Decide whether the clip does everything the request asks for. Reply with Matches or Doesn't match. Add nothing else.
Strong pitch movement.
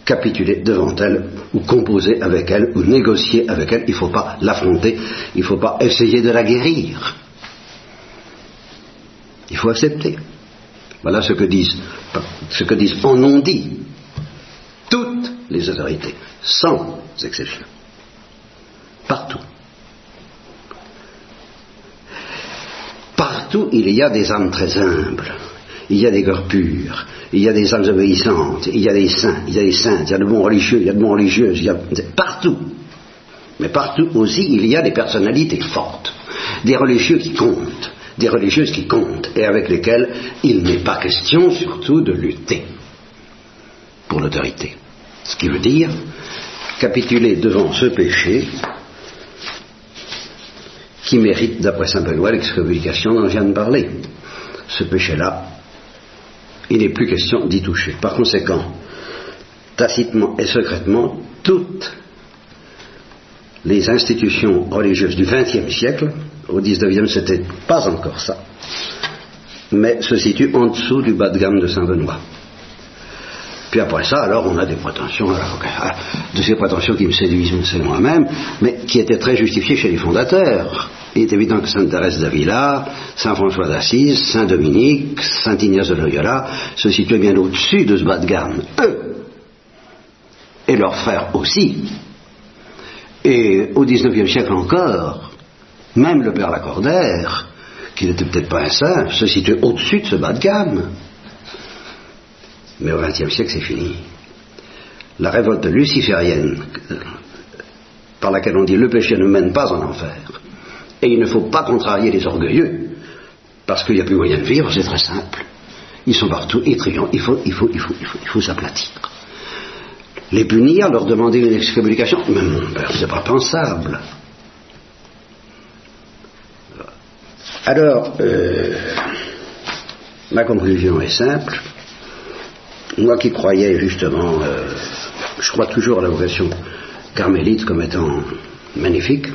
Doesn't match